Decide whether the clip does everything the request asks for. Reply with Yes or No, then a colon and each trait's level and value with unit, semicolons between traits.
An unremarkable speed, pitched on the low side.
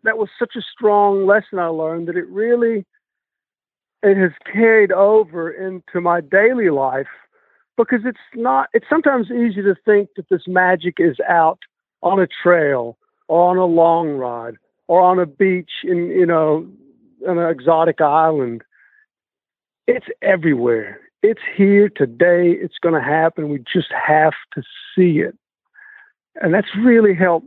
No: average, 150 wpm; medium, 185 Hz